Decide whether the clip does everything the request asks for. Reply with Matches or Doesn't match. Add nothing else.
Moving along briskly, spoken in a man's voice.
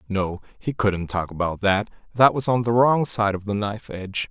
Matches